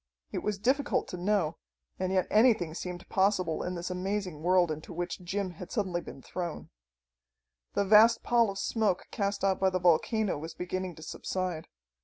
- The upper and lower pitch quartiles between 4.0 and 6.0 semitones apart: No, narrow, 2.6 semitones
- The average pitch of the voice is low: No, medium, 185 Hz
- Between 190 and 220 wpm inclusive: No, average, 175 wpm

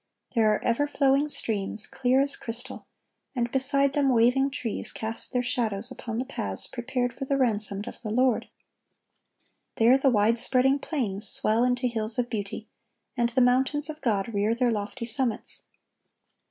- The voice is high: Yes, high, 245 Hz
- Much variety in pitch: No, average, 3.2 semitones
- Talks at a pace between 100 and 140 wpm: No, average, 165 wpm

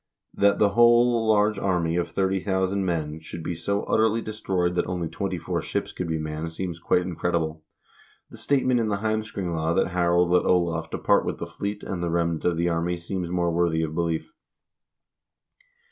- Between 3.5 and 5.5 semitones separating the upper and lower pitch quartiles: No, average, 3.1 semitones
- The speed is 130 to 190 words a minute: Yes, average, 185 wpm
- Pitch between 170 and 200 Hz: No, very low, 90 Hz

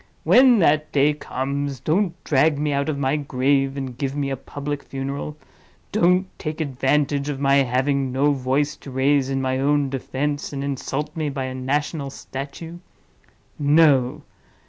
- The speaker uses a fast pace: No, average, 160 wpm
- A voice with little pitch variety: Yes, narrow, 1.7 semitones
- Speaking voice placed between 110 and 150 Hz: Yes, medium, 140 Hz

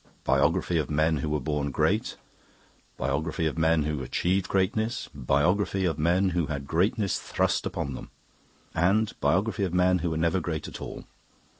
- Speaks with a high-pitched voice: No, very low, 80 Hz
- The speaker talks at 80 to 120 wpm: No, average, 165 wpm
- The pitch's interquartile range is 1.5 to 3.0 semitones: No, average, 3.8 semitones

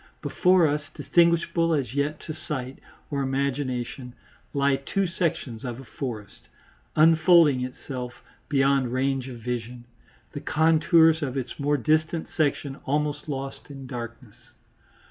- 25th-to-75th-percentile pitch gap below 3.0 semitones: No, average, 3.6 semitones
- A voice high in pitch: No, medium, 140 Hz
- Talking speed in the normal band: No, slow, 125 wpm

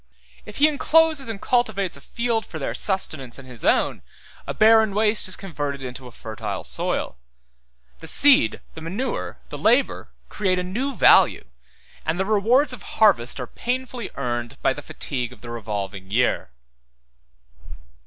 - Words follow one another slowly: No, average, 155 wpm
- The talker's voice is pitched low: No, high, 190 Hz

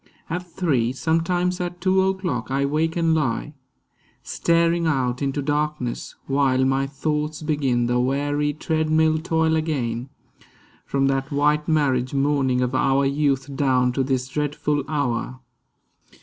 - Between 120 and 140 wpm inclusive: Yes, slow, 135 wpm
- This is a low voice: No, medium, 145 Hz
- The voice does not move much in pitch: No, average, 3.1 semitones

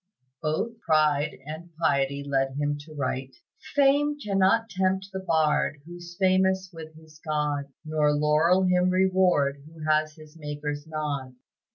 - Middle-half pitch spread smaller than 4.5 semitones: Yes, average, 4.1 semitones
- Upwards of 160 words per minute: No, average, 140 wpm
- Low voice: No, medium, 155 Hz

